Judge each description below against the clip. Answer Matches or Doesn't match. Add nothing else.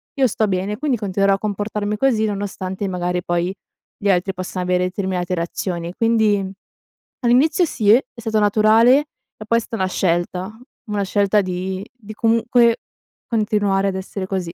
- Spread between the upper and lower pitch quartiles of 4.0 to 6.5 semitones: Doesn't match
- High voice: Matches